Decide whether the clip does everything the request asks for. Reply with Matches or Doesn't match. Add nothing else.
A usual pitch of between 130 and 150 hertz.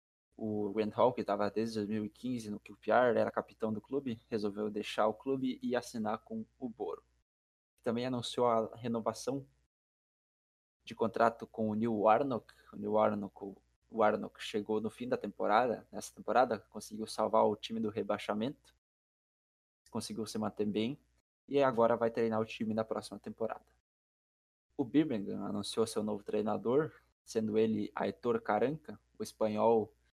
Doesn't match